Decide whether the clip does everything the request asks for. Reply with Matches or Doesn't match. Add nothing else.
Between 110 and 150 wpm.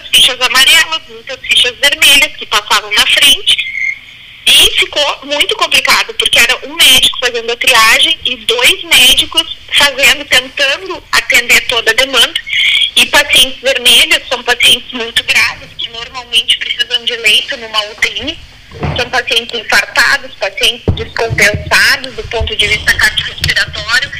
Matches